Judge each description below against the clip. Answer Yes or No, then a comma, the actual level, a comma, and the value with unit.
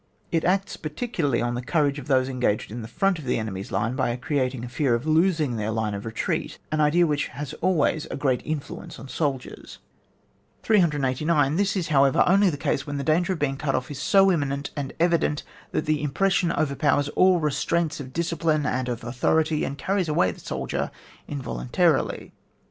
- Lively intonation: No, average, 4.3 semitones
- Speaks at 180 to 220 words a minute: Yes, average, 195 wpm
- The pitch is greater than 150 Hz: No, medium, 145 Hz